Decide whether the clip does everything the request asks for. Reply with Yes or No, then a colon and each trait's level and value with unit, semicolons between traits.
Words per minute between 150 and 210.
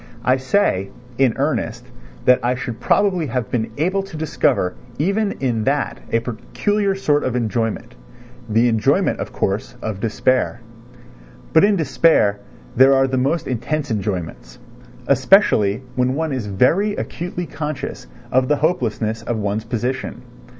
No: average, 140 wpm